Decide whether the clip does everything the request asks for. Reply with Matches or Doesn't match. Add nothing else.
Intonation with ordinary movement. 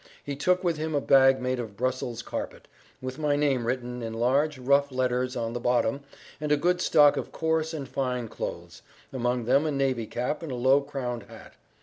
Matches